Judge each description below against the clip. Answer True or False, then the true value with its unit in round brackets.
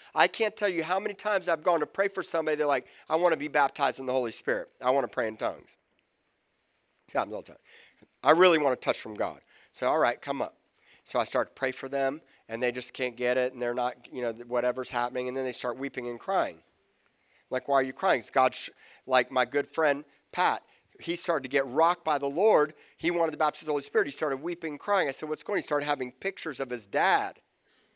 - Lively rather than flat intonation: False (4.2 semitones)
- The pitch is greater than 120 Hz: True (140 Hz)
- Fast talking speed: True (255 wpm)